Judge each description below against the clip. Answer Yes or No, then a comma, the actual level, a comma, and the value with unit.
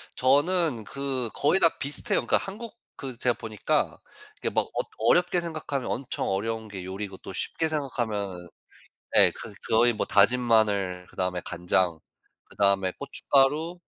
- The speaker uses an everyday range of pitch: No, wide, 6.3 semitones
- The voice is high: No, low, 120 Hz